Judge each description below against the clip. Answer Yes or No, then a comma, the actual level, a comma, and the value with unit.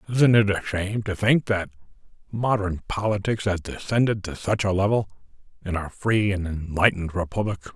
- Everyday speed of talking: Yes, average, 160 wpm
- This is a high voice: No, low, 100 Hz